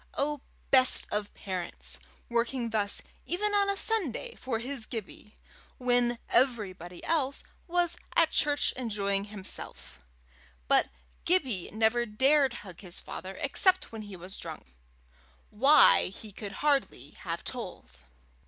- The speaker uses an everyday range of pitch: No, wide, 5.9 semitones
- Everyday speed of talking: No, slow, 125 wpm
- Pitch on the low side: No, high, 235 Hz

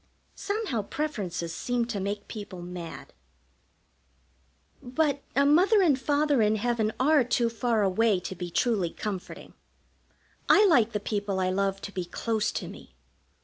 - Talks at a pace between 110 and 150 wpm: Yes, average, 145 wpm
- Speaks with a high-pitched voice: Yes, high, 220 Hz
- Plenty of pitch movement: Yes, wide, 5.7 semitones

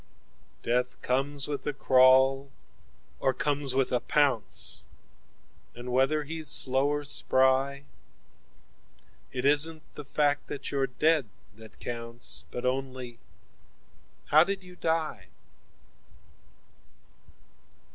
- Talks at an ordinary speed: No, slow, 100 wpm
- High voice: No, low, 135 Hz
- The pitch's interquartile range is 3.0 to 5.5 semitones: No, narrow, 2.6 semitones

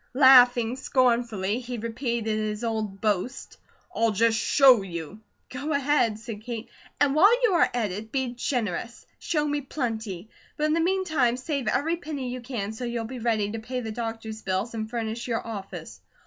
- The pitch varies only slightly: No, average, 3.2 semitones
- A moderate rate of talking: Yes, average, 175 wpm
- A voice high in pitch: Yes, high, 235 Hz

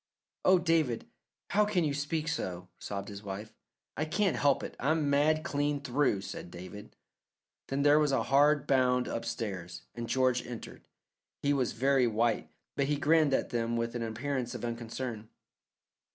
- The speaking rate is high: No, average, 165 wpm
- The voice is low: Yes, low, 130 Hz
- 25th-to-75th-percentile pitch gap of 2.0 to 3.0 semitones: No, average, 4.2 semitones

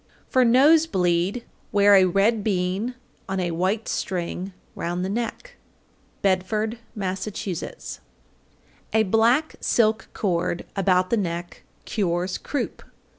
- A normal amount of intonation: Yes, average, 3.6 semitones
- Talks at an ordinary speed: No, slow, 120 wpm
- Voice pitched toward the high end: Yes, high, 195 Hz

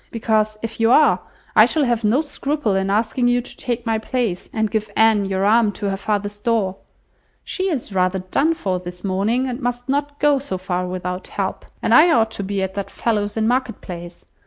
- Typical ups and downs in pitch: Yes, average, 4.0 semitones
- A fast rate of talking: Yes, fast, 215 wpm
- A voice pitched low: No, high, 220 Hz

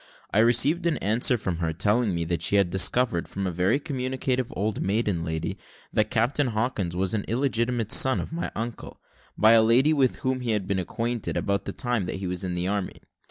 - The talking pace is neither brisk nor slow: No, fast, 210 wpm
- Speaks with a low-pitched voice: Yes, low, 110 Hz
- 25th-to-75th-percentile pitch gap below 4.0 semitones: No, average, 4.7 semitones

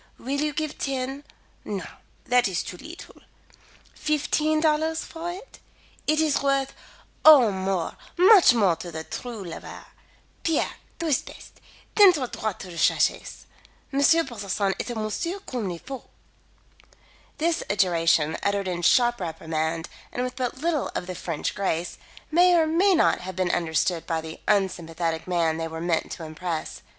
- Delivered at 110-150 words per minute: No, average, 160 wpm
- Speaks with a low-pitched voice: No, high, 215 Hz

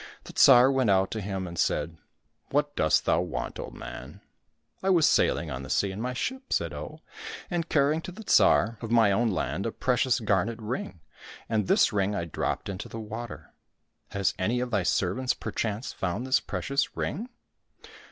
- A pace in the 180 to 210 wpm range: Yes, average, 200 wpm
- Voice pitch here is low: Yes, low, 115 Hz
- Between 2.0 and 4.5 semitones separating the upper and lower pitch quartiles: No, average, 5.3 semitones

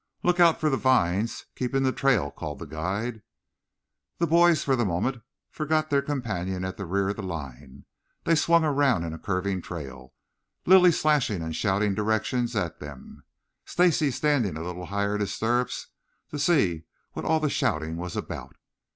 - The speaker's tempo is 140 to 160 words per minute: No, average, 175 wpm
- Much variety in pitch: Yes, wide, 8.4 semitones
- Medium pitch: No, low, 110 Hz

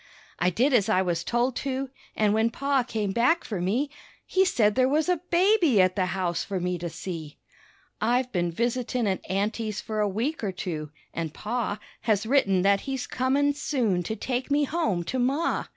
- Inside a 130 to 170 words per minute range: No, average, 195 wpm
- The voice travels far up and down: Yes, wide, 5.9 semitones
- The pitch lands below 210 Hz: No, high, 225 Hz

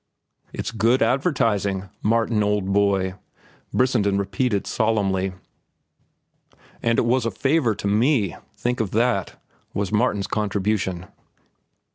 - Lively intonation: No, average, 3.1 semitones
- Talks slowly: Yes, slow, 105 wpm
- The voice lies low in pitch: Yes, low, 105 Hz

